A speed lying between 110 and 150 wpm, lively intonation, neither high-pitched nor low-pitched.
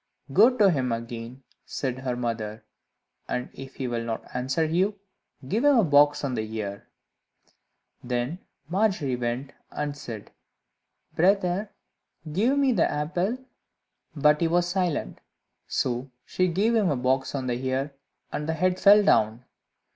Yes: average, 145 wpm; wide, 6.9 semitones; medium, 145 Hz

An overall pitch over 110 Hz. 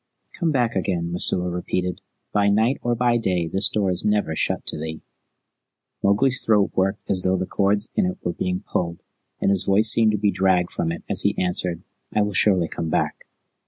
No: very low, 95 Hz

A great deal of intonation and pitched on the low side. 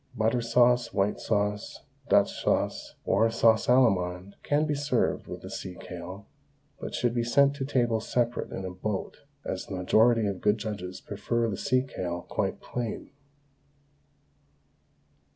No: average, 3.9 semitones; low, 110 Hz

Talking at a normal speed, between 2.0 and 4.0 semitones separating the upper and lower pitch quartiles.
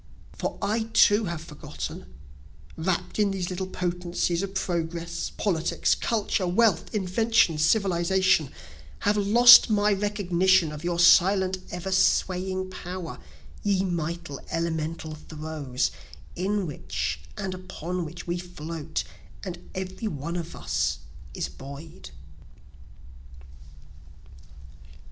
No: slow, 110 wpm; average, 2.7 semitones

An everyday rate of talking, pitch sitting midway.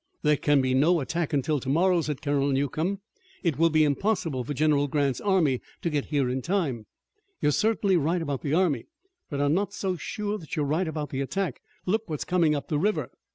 No: fast, 210 wpm; medium, 155 Hz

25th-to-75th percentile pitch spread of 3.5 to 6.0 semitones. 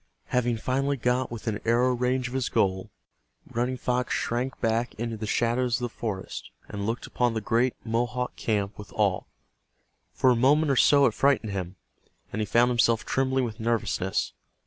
No: narrow, 2.4 semitones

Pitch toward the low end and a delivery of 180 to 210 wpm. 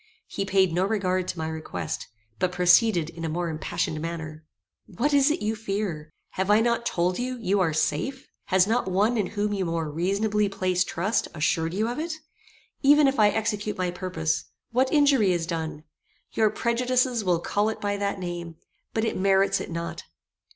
No: high, 195 Hz; average, 185 wpm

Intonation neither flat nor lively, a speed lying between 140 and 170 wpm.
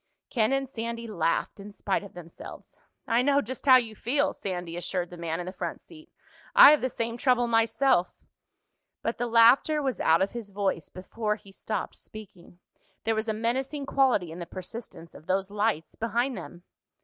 No: average, 4.8 semitones; average, 185 wpm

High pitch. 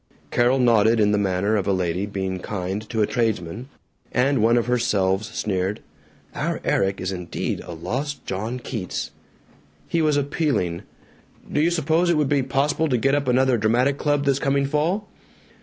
No: low, 120 Hz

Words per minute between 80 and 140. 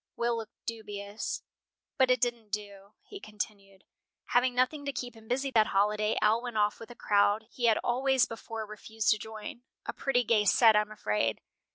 No: average, 190 wpm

